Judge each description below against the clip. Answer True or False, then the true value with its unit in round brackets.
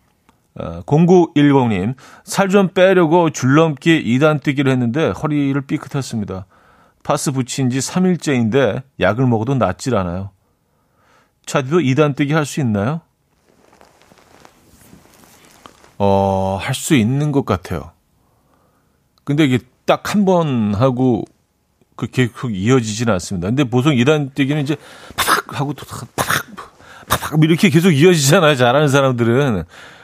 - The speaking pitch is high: False (135 Hz)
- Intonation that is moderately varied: True (4.8 semitones)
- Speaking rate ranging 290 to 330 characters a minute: False (245 characters per minute)